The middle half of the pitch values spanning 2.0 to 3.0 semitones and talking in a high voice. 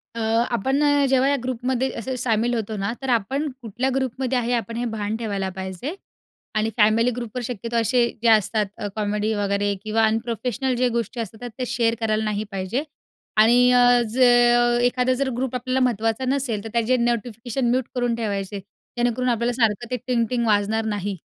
Yes: narrow, 2.6 semitones; high, 235 Hz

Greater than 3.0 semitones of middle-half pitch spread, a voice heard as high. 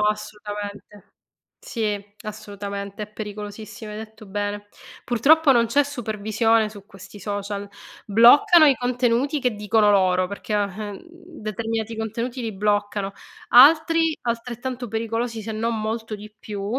No: narrow, 2.5 semitones; high, 215 Hz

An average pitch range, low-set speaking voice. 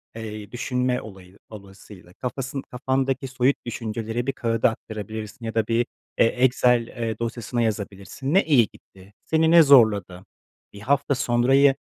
Yes: average, 3.5 semitones; low, 115 Hz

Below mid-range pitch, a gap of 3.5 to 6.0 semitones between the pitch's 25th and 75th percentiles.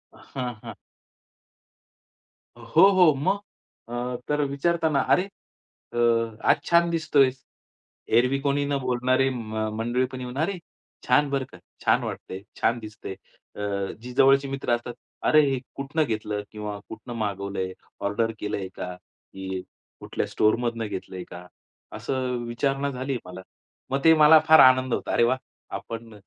Yes: low, 125 Hz; average, 3.9 semitones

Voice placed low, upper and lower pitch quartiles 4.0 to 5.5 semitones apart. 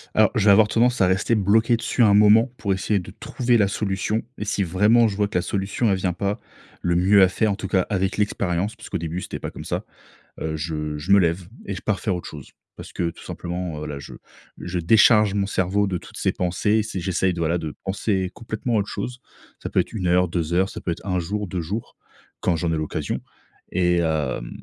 No: very low, 95 Hz; average, 3.3 semitones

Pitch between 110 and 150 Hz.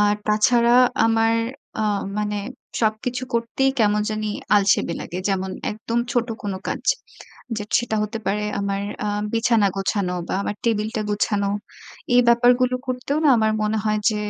No: high, 215 Hz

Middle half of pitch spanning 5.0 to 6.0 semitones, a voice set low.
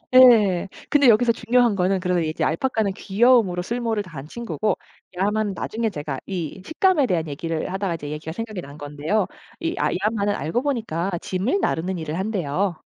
No: wide, 5.4 semitones; high, 195 Hz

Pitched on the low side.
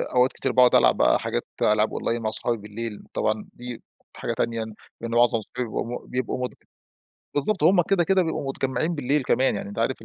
Yes: low, 125 Hz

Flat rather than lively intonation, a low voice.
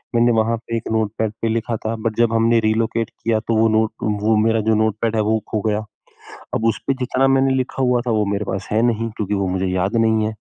Yes: narrow, 1.2 semitones; low, 110 Hz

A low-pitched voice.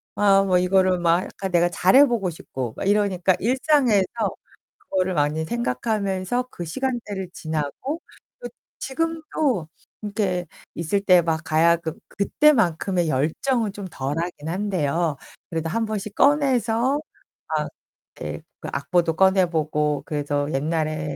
No: medium, 185 Hz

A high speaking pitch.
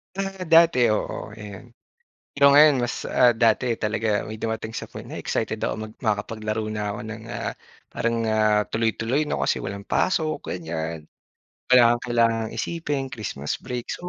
No: low, 115 Hz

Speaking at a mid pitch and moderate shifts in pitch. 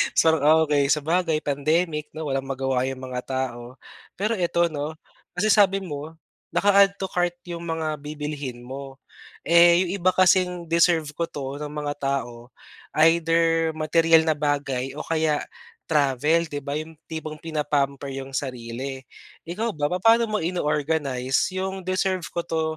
Yes: medium, 155 Hz; average, 3.6 semitones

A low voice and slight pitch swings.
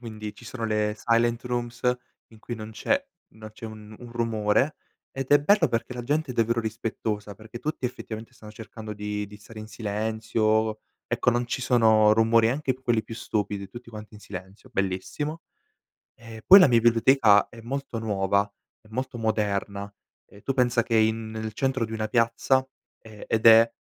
Yes: low, 115 Hz; narrow, 2.0 semitones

